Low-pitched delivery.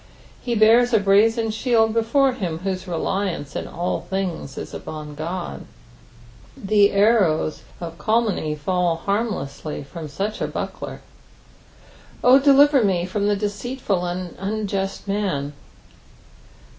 No: high, 195 Hz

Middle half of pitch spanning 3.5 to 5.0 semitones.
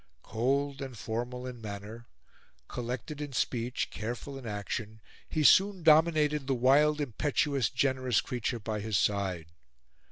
Yes: average, 4.4 semitones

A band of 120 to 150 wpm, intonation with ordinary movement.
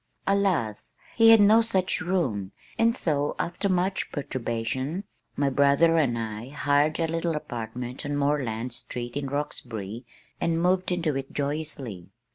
No: average, 140 wpm; wide, 6.1 semitones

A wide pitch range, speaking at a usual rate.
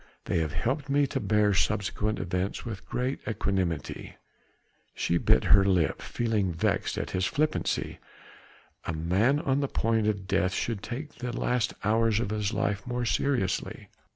No: average, 4.3 semitones; average, 155 wpm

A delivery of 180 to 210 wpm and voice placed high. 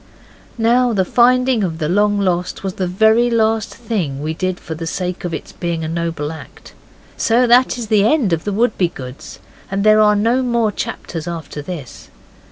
Yes: average, 185 wpm; high, 195 Hz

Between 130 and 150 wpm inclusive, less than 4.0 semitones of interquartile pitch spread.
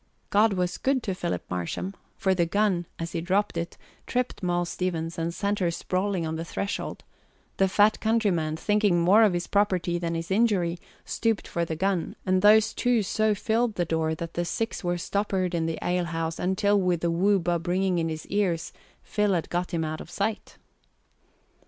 No: average, 190 wpm; average, 3.3 semitones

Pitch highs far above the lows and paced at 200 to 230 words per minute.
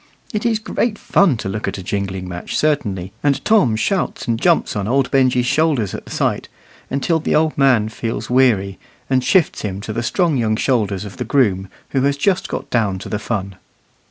Yes: wide, 6.0 semitones; fast, 205 wpm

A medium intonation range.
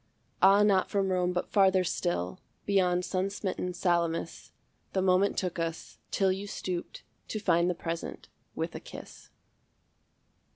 No: narrow, 2.0 semitones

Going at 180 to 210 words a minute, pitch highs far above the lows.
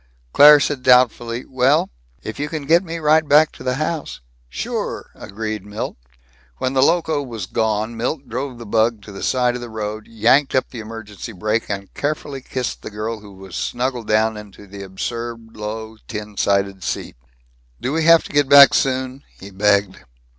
No: average, 185 wpm; average, 4.3 semitones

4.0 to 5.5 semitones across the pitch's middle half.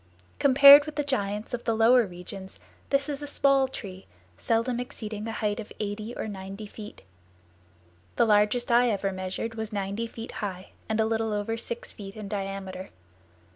No: average, 3.1 semitones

